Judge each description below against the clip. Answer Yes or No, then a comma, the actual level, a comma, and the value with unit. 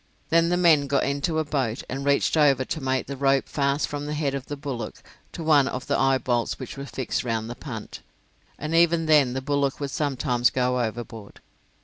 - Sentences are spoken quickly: Yes, fast, 210 wpm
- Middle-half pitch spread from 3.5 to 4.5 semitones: No, average, 2.7 semitones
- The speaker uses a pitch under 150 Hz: Yes, medium, 140 Hz